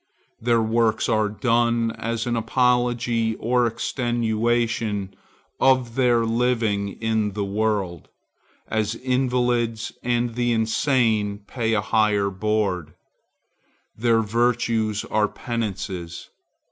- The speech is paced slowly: Yes, slow, 95 wpm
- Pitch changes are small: Yes, narrow, 2.0 semitones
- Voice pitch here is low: Yes, low, 115 Hz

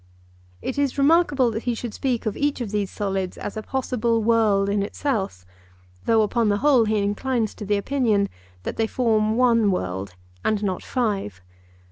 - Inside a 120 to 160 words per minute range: No, average, 175 wpm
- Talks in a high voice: Yes, high, 220 Hz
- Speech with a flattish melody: No, average, 3.6 semitones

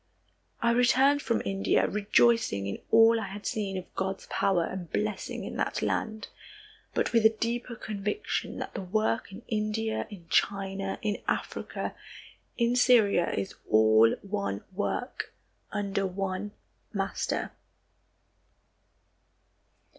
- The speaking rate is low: Yes, slow, 125 wpm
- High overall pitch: Yes, high, 205 Hz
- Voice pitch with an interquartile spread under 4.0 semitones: Yes, average, 2.7 semitones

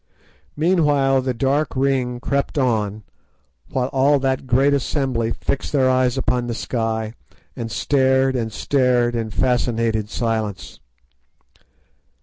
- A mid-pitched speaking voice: No, low, 125 Hz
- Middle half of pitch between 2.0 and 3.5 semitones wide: Yes, average, 2.8 semitones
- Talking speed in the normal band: No, slow, 120 wpm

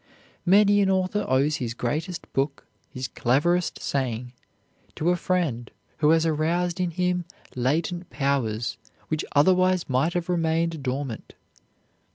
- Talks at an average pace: No, slow, 130 wpm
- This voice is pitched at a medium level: Yes, medium, 160 Hz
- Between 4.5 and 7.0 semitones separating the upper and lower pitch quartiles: Yes, average, 5.2 semitones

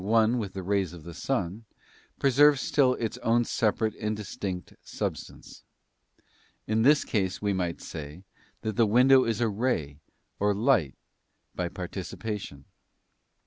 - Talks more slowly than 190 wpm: Yes, slow, 135 wpm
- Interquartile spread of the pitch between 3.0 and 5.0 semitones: Yes, average, 4.2 semitones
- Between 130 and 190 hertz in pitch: No, low, 105 Hz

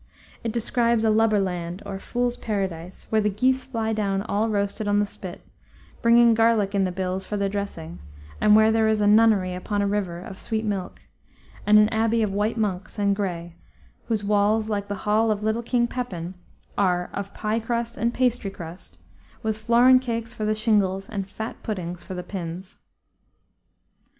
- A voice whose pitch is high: Yes, high, 210 Hz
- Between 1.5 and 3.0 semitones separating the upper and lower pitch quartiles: Yes, narrow, 2.6 semitones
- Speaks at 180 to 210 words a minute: Yes, average, 185 wpm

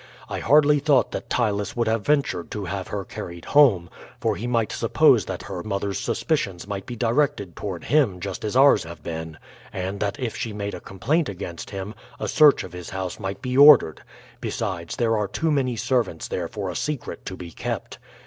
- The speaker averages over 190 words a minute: Yes, average, 200 wpm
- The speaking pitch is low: Yes, low, 100 Hz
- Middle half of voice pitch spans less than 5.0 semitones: No, wide, 5.4 semitones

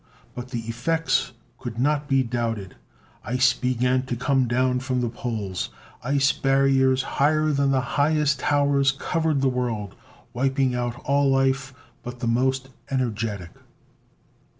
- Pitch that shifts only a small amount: Yes, narrow, 2.2 semitones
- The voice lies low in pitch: Yes, low, 130 Hz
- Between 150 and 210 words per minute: No, slow, 135 wpm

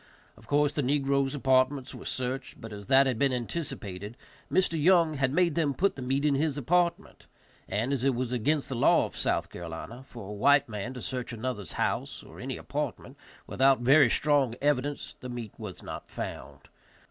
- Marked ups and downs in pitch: No, average, 3.3 semitones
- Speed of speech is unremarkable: Yes, average, 190 wpm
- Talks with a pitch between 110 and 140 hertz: Yes, low, 135 Hz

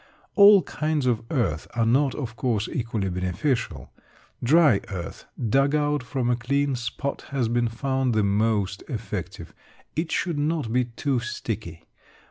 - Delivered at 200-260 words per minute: No, average, 145 wpm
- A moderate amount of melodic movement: Yes, average, 4.5 semitones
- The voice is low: Yes, low, 120 Hz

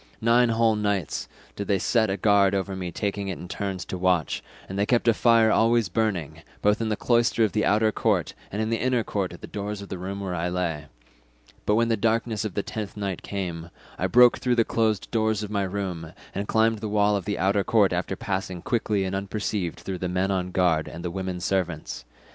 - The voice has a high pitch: No, low, 100 Hz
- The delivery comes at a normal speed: No, fast, 230 wpm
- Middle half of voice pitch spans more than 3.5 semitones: No, average, 3.0 semitones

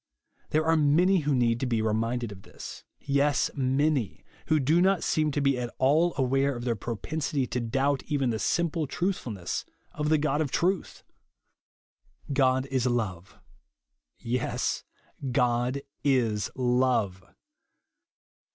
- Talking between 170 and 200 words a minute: No, average, 140 wpm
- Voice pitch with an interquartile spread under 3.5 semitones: No, average, 3.8 semitones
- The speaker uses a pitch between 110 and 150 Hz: Yes, low, 135 Hz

